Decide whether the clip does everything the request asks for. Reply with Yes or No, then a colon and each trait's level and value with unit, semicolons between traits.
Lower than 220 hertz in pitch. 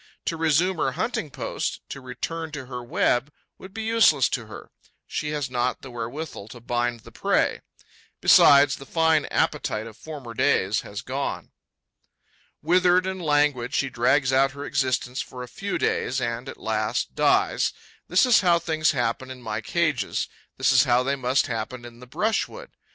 Yes: low, 135 Hz